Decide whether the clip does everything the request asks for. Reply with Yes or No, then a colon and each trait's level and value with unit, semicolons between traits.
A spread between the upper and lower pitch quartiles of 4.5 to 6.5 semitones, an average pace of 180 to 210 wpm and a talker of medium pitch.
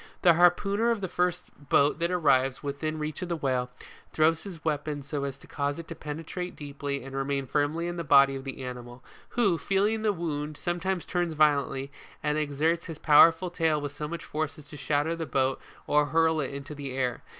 No: average, 3.2 semitones; fast, 205 wpm; medium, 150 Hz